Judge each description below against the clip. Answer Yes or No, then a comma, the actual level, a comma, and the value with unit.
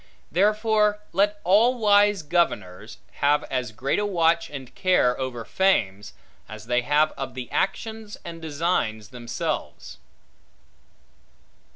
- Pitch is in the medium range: Yes, medium, 160 Hz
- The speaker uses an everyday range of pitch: No, wide, 8.6 semitones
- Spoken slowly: Yes, slow, 115 wpm